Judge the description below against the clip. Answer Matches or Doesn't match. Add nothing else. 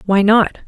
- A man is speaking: Doesn't match